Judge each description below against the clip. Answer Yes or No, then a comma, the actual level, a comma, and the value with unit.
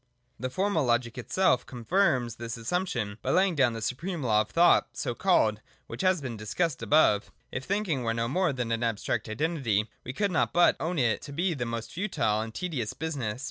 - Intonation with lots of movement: Yes, wide, 7.1 semitones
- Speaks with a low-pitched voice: Yes, low, 130 Hz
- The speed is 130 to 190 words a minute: No, average, 200 wpm